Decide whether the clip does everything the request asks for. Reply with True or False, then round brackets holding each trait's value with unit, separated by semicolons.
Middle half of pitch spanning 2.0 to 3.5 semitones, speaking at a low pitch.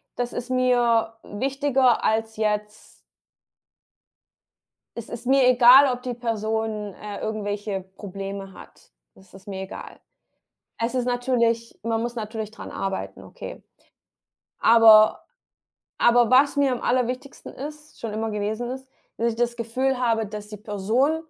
False (2.8 semitones; 230 Hz)